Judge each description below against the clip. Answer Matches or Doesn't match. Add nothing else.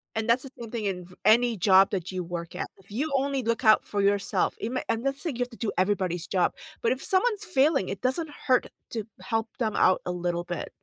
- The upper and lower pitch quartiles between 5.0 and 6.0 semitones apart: Matches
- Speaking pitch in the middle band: Doesn't match